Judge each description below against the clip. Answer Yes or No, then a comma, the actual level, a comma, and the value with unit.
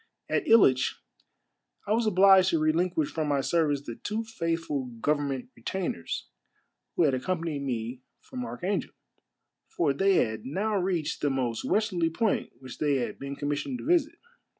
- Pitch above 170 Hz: No, medium, 165 Hz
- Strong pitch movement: Yes, wide, 6.0 semitones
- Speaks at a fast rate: No, average, 155 wpm